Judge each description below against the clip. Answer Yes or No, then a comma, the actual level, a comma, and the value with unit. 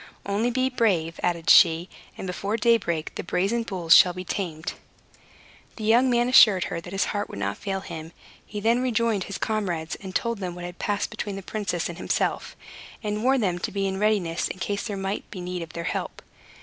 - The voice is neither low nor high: No, high, 195 Hz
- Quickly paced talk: Yes, fast, 210 wpm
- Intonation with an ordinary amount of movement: Yes, average, 3.7 semitones